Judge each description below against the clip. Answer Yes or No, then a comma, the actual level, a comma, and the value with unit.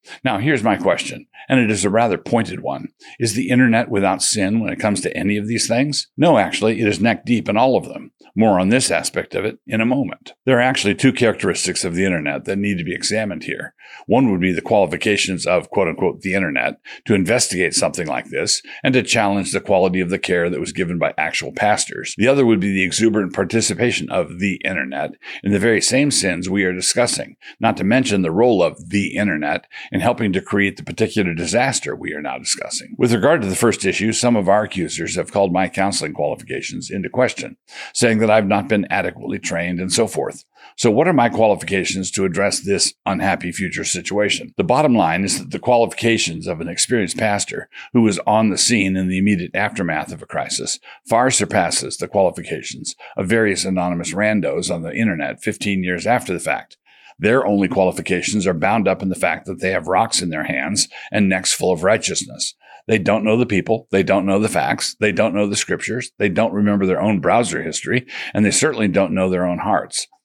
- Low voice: Yes, low, 100 Hz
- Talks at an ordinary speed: No, fast, 215 wpm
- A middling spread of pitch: Yes, average, 3.1 semitones